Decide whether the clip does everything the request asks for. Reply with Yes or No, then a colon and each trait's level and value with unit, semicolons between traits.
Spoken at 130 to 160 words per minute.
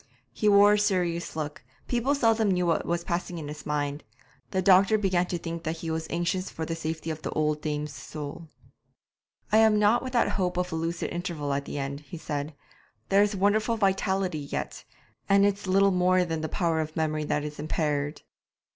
No: average, 200 wpm